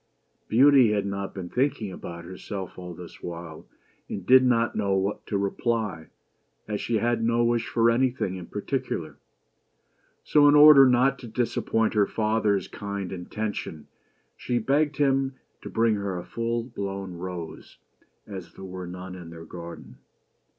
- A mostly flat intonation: No, average, 4.3 semitones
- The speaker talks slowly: No, average, 155 wpm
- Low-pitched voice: Yes, low, 105 Hz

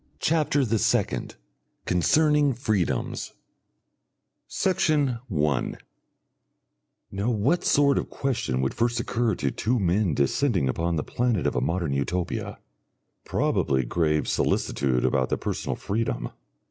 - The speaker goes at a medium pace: No, slow, 120 wpm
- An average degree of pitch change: No, wide, 9.0 semitones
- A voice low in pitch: Yes, low, 100 Hz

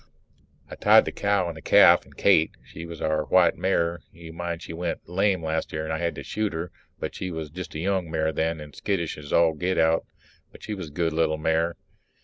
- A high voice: No, very low, 85 Hz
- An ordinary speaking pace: No, fast, 235 wpm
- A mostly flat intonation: Yes, narrow, 1.9 semitones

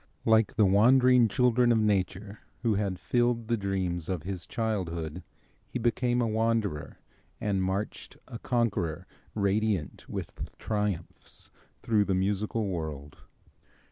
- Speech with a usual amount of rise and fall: Yes, average, 3.5 semitones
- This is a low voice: Yes, low, 105 Hz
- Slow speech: Yes, slow, 125 wpm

